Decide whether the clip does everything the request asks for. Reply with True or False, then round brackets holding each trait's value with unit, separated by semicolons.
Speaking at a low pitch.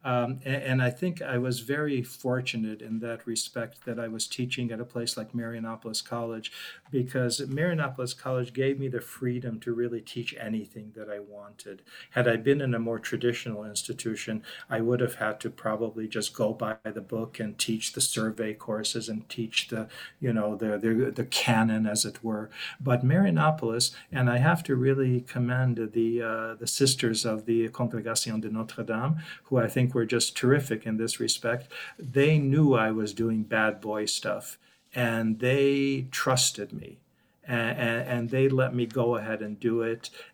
True (115 Hz)